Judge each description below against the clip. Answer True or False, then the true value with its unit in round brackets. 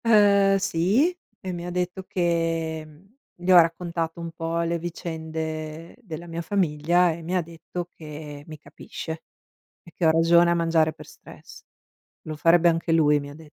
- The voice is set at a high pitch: False (165 Hz)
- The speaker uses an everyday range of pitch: False (1.8 semitones)